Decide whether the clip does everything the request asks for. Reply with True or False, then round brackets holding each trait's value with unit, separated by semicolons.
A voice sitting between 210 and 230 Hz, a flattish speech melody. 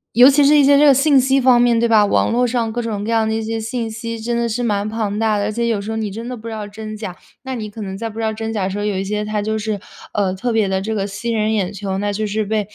True (220 Hz; 2.2 semitones)